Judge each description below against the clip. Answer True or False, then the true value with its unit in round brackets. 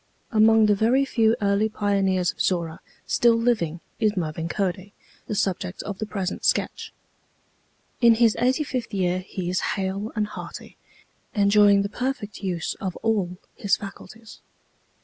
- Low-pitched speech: False (205 Hz)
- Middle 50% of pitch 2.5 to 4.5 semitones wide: True (3.0 semitones)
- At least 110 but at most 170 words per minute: True (150 wpm)